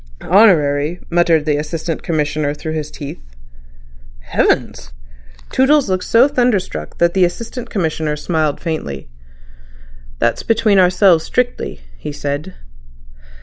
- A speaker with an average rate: No, slow, 110 wpm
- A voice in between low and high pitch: Yes, medium, 165 Hz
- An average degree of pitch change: Yes, average, 4.7 semitones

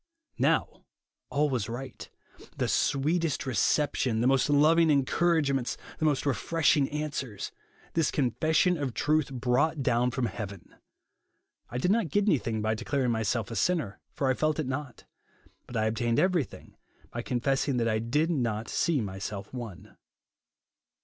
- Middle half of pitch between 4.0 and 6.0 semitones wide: Yes, average, 4.6 semitones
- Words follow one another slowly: No, average, 150 wpm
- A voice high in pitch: No, low, 135 Hz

